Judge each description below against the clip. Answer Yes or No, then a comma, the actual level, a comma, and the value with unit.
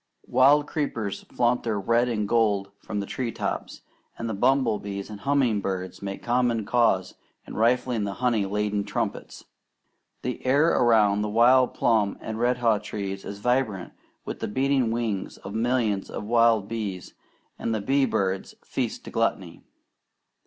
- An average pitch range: Yes, average, 3.3 semitones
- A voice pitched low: Yes, low, 110 Hz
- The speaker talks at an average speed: Yes, average, 150 wpm